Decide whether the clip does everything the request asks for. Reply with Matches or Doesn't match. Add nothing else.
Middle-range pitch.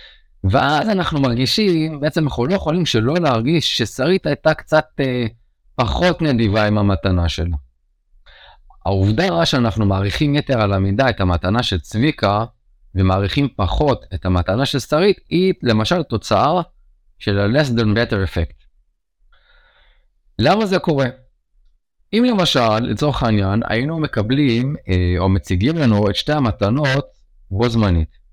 Doesn't match